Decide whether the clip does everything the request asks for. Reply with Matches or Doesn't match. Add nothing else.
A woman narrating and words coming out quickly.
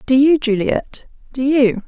Doesn't match